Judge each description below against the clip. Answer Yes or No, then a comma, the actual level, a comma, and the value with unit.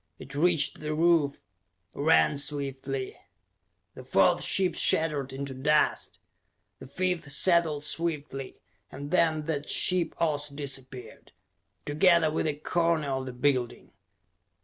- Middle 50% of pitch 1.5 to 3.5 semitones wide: Yes, average, 2.9 semitones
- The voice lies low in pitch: No, medium, 150 Hz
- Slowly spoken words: Yes, slow, 120 wpm